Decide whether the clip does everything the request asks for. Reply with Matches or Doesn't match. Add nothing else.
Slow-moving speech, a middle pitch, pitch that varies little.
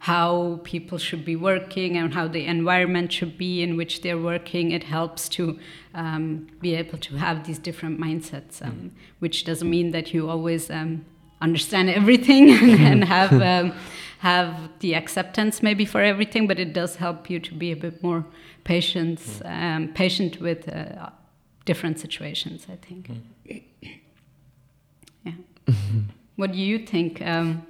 Doesn't match